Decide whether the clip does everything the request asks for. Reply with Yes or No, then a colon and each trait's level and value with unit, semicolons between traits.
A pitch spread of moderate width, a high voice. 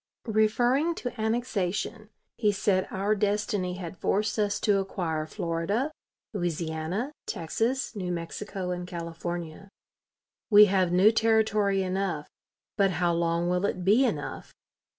Yes: average, 3.5 semitones; high, 195 Hz